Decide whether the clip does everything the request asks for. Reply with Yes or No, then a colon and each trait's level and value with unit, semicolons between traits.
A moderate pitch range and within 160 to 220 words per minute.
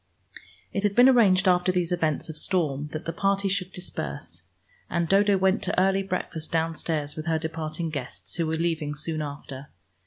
Yes: average, 3.5 semitones; average, 180 wpm